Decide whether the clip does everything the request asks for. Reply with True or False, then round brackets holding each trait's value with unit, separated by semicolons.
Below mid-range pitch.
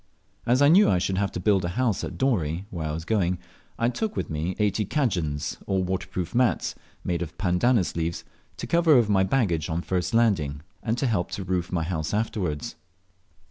True (95 Hz)